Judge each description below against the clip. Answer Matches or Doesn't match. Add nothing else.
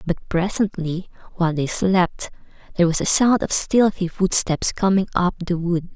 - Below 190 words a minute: Matches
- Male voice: Doesn't match